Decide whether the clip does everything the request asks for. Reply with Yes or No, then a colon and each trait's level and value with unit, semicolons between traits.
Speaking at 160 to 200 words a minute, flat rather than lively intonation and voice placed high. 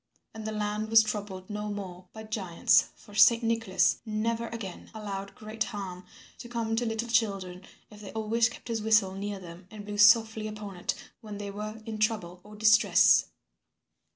Yes: average, 180 wpm; narrow, 2.0 semitones; high, 215 Hz